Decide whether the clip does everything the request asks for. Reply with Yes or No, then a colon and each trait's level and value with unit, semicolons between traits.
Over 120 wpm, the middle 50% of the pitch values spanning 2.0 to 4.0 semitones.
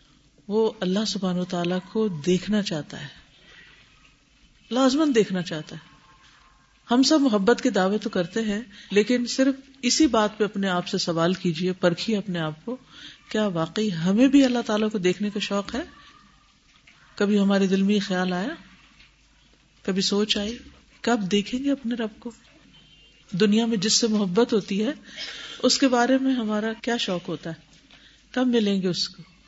No: average, 165 wpm; average, 4.4 semitones